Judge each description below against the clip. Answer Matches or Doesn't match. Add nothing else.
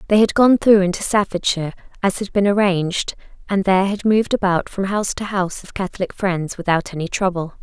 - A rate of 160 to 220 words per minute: Matches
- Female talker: Matches